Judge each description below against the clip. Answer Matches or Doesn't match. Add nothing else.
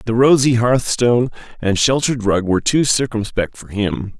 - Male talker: Matches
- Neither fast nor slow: Matches